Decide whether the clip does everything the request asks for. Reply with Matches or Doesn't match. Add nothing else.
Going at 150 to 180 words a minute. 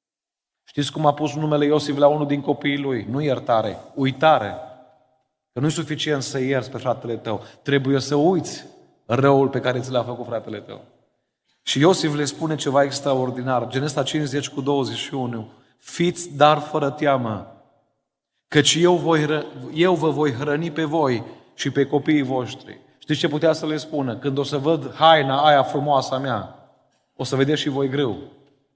Matches